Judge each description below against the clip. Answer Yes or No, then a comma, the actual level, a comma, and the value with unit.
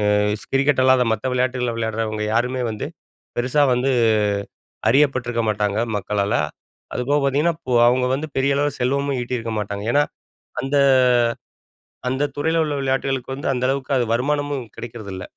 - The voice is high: No, low, 130 Hz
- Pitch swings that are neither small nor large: Yes, average, 3.2 semitones